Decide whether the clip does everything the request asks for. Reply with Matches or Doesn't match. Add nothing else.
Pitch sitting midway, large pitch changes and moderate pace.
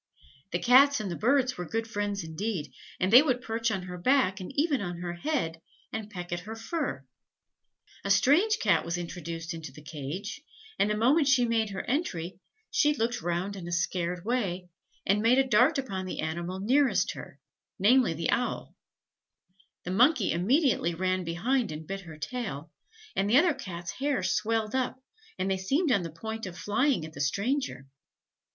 Doesn't match